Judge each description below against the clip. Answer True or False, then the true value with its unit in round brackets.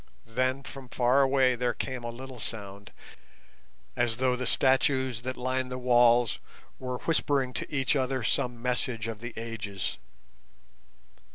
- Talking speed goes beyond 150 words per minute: False (145 wpm)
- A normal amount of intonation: False (1.8 semitones)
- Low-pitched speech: True (125 Hz)